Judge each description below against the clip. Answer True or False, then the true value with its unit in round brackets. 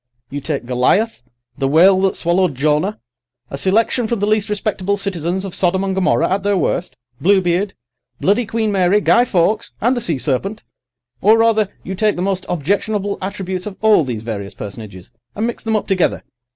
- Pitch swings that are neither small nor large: True (3.6 semitones)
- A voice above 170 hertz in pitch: True (190 Hz)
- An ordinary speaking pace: True (180 wpm)